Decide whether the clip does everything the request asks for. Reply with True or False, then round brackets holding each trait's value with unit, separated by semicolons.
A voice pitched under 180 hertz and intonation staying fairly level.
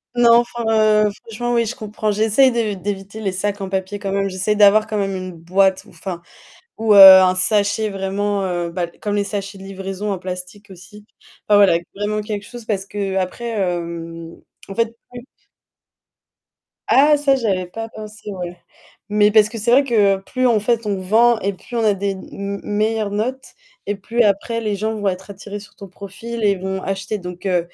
False (205 Hz; 2.3 semitones)